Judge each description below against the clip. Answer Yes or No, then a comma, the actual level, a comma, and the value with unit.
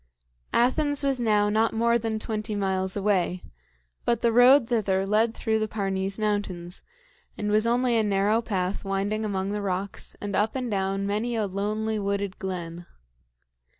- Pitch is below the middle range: No, high, 210 Hz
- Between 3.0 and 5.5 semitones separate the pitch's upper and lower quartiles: No, narrow, 2.4 semitones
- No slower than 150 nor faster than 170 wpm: Yes, average, 160 wpm